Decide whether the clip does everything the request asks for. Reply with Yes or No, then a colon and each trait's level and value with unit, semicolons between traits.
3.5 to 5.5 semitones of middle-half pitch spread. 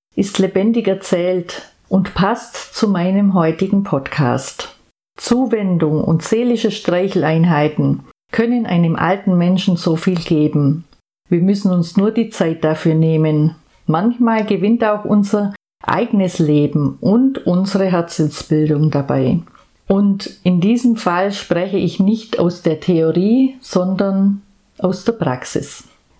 Yes: average, 3.8 semitones